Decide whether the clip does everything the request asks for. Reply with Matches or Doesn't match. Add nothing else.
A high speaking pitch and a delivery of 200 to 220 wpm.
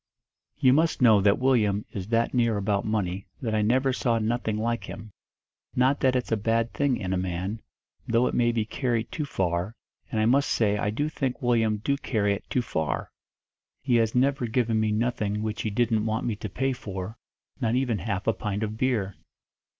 Doesn't match